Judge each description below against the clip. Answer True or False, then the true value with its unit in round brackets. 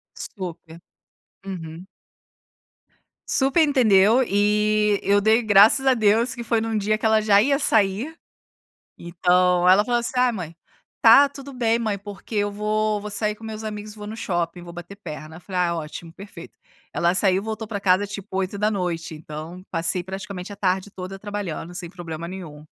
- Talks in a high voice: True (200 Hz)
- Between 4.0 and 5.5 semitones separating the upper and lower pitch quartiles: False (3.4 semitones)